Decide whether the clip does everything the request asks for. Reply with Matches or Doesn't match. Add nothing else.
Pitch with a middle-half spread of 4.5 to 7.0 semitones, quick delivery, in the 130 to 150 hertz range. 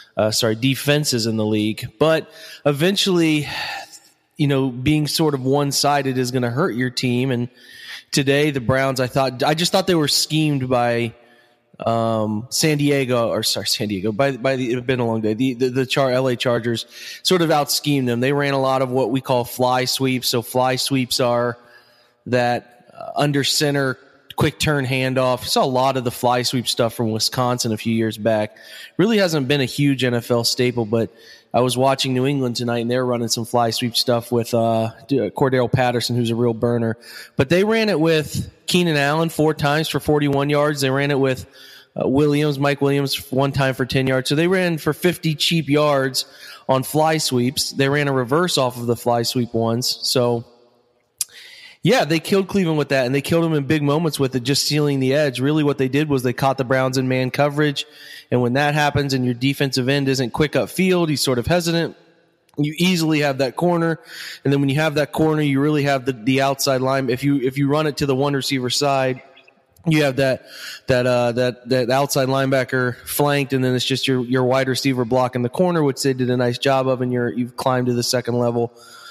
Doesn't match